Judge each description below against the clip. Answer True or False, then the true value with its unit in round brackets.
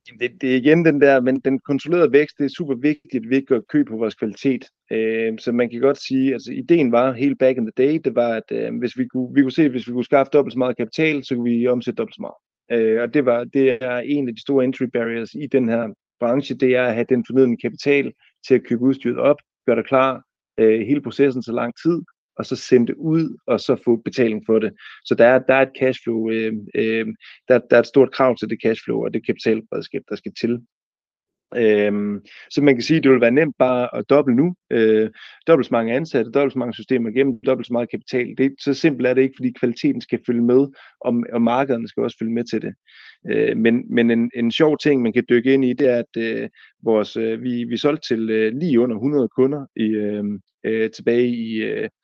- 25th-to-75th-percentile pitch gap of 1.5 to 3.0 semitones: True (2.7 semitones)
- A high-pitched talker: False (125 Hz)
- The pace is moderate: False (245 wpm)